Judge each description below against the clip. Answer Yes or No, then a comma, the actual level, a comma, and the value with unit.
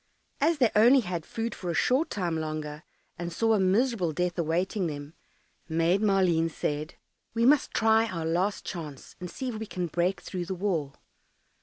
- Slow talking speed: No, average, 180 wpm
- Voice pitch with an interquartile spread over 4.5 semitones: Yes, average, 5.1 semitones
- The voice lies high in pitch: No, medium, 180 Hz